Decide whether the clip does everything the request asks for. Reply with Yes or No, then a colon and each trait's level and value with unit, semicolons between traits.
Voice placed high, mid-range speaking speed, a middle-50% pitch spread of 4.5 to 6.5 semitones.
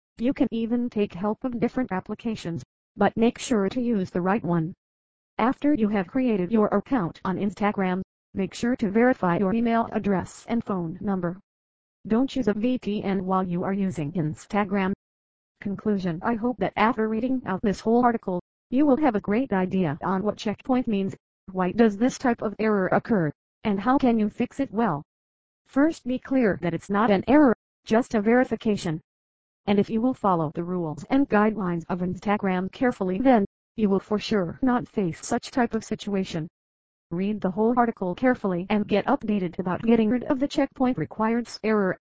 No: high, 205 Hz; average, 180 wpm; average, 4.1 semitones